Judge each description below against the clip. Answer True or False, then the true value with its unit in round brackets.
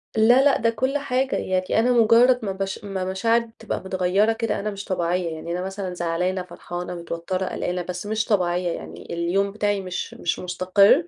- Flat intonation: False (3.8 semitones)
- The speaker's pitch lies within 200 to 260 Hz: False (190 Hz)